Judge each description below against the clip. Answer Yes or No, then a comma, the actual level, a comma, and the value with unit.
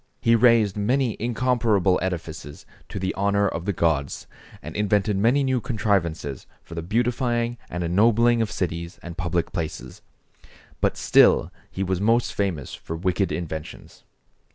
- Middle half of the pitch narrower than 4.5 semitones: No, average, 5.3 semitones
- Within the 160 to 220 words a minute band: No, average, 145 wpm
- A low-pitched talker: Yes, low, 100 Hz